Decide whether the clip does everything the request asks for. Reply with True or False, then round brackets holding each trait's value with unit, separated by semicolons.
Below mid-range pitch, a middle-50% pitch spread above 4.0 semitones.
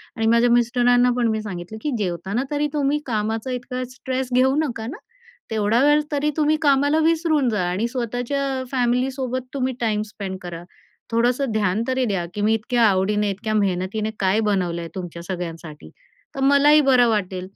False (235 Hz; 4.4 semitones)